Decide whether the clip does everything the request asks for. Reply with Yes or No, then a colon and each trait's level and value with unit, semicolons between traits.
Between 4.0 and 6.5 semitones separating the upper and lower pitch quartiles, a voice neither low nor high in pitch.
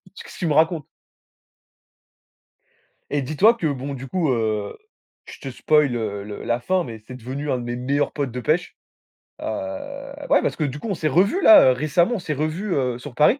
Yes: average, 4.7 semitones; medium, 145 Hz